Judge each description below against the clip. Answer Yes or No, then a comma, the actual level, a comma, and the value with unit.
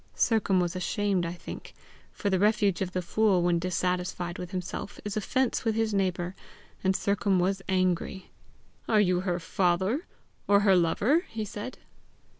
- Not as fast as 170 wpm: Yes, average, 160 wpm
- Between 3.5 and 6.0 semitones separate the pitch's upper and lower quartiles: No, narrow, 2.5 semitones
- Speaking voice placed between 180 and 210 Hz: Yes, high, 190 Hz